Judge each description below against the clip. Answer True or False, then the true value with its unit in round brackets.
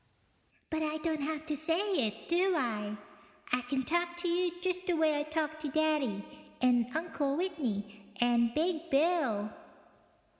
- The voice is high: True (310 Hz)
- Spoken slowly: False (155 wpm)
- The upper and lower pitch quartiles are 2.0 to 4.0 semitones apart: False (5.5 semitones)